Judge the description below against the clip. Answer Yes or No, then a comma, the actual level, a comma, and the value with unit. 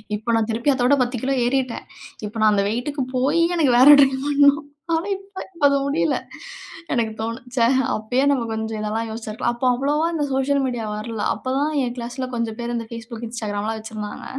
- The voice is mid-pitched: No, high, 240 Hz